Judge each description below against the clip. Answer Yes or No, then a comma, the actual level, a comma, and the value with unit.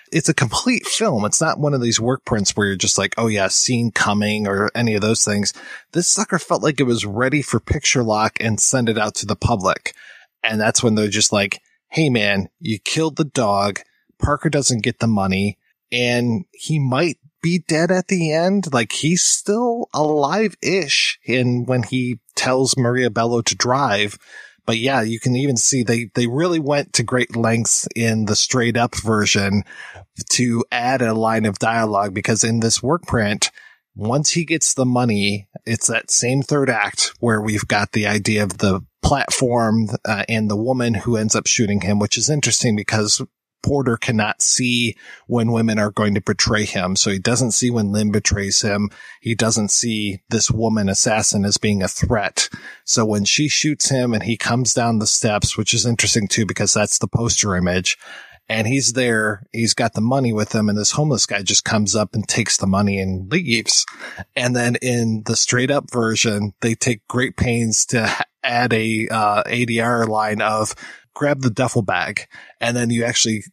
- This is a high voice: No, low, 115 Hz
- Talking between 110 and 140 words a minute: No, average, 190 wpm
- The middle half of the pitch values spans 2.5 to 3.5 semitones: Yes, average, 3.2 semitones